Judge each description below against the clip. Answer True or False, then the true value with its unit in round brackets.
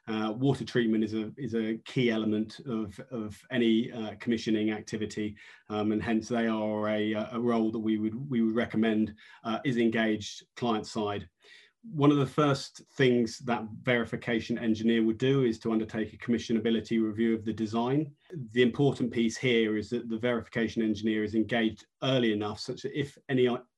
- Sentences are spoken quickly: False (175 wpm)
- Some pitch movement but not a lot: False (1.9 semitones)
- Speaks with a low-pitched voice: True (115 Hz)